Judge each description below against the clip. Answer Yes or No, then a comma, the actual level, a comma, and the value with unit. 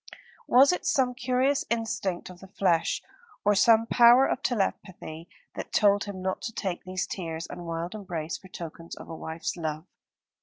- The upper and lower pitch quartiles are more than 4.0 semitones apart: Yes, wide, 5.6 semitones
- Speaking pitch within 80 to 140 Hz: No, high, 190 Hz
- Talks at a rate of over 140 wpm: Yes, average, 175 wpm